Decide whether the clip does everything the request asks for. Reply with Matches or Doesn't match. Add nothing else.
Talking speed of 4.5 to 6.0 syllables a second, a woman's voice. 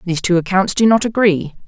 Doesn't match